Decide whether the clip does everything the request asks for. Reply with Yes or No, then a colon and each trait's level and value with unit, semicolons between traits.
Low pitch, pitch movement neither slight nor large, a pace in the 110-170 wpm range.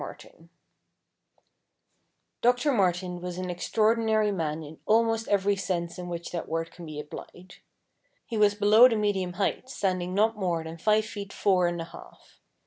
No: high, 190 Hz; average, 3.7 semitones; average, 160 wpm